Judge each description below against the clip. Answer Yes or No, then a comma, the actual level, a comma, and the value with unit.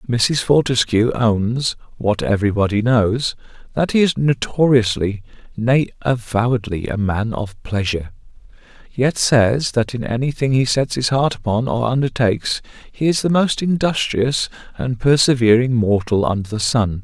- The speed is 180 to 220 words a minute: No, average, 145 wpm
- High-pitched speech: No, low, 120 Hz